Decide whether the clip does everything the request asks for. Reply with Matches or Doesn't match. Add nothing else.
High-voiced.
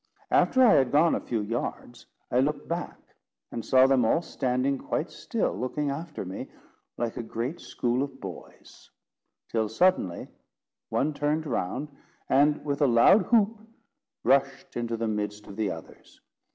Doesn't match